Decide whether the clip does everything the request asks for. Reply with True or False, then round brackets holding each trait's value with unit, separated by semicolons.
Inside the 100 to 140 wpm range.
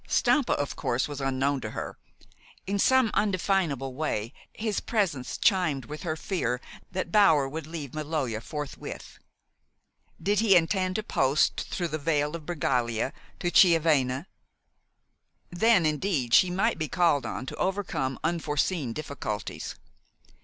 True (135 wpm)